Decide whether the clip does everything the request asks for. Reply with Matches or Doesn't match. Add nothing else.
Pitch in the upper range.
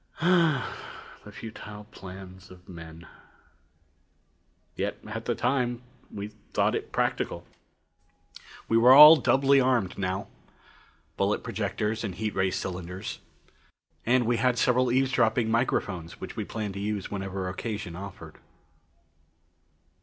Doesn't match